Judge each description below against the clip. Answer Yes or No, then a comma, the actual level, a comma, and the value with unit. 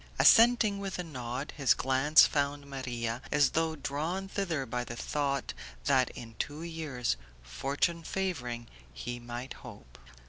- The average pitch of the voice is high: No, medium, 140 Hz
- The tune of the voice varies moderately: Yes, average, 4.8 semitones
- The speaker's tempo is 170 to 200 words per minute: No, average, 140 wpm